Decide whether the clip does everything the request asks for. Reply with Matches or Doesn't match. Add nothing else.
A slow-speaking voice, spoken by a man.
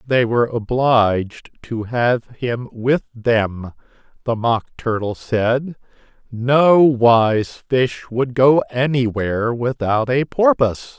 Matches